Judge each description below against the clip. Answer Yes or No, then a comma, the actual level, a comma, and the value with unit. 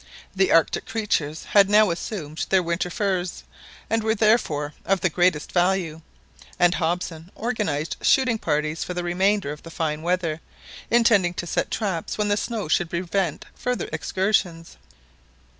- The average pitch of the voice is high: No, medium, 180 Hz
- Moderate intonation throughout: Yes, average, 3.9 semitones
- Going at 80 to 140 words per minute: No, average, 150 wpm